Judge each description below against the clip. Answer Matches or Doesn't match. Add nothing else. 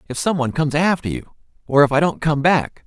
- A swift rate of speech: Matches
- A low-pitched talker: Doesn't match